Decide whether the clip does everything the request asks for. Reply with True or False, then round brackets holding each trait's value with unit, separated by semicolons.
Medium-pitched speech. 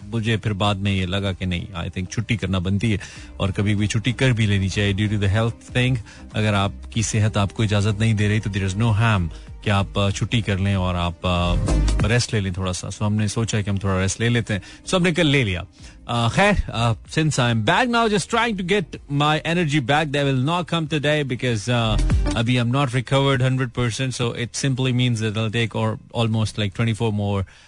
False (110 Hz)